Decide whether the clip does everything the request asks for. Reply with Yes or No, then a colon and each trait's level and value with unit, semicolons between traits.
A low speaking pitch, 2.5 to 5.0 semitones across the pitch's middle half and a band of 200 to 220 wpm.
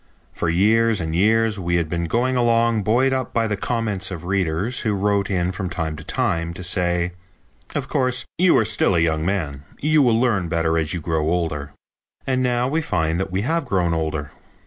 No: very low, 95 Hz; wide, 5.6 semitones; fast, 205 wpm